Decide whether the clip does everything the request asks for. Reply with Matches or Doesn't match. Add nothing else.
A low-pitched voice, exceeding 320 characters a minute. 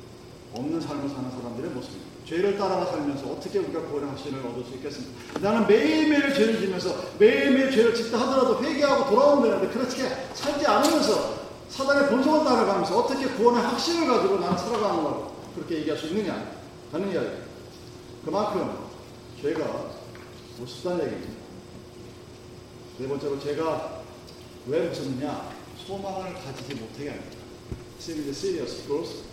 Doesn't match